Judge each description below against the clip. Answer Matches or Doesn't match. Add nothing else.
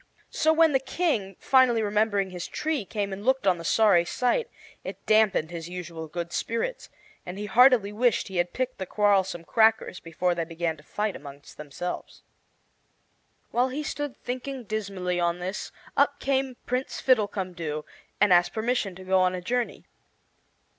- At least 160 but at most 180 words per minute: Matches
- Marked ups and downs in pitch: Matches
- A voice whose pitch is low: Doesn't match